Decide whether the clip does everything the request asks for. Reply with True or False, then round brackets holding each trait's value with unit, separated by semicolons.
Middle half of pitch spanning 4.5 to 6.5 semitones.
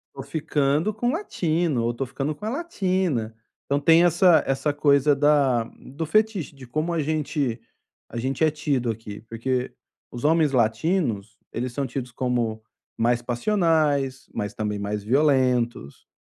True (5.0 semitones)